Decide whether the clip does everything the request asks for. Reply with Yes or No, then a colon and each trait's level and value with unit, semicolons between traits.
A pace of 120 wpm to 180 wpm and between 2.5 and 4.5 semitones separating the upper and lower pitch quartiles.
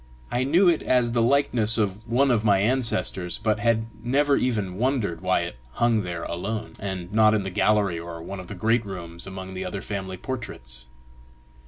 No: average, 190 wpm; average, 4.2 semitones